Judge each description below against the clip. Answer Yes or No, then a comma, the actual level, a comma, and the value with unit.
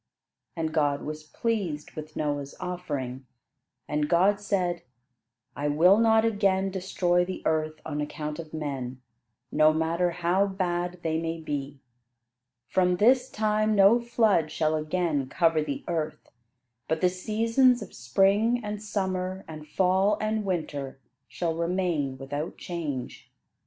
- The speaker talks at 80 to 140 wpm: Yes, slow, 135 wpm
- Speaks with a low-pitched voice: No, medium, 175 Hz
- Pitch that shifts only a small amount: No, average, 4.2 semitones